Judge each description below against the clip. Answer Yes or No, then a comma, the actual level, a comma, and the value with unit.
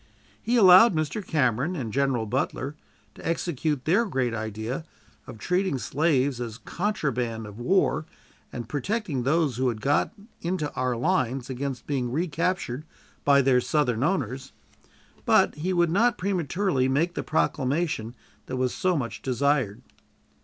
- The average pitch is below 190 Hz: Yes, medium, 140 Hz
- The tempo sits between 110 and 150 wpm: Yes, average, 140 wpm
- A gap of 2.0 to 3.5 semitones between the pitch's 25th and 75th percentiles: No, wide, 5.4 semitones